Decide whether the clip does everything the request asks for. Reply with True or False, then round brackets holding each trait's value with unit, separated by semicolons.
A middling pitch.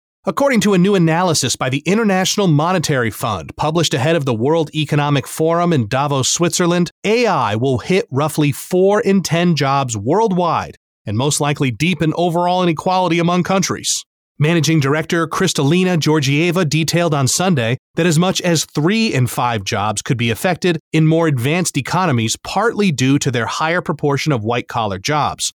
True (160 Hz)